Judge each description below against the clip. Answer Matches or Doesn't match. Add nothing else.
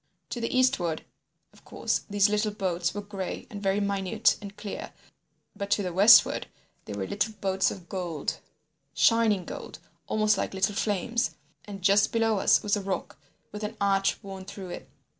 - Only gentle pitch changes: Matches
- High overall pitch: Matches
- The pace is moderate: Matches